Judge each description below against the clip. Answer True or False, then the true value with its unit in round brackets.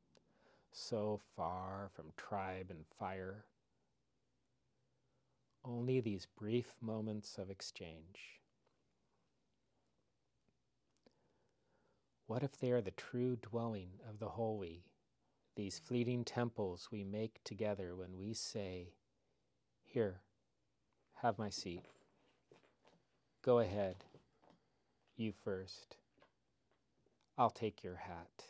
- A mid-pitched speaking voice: False (105 Hz)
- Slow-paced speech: True (90 wpm)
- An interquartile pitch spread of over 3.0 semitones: True (3.4 semitones)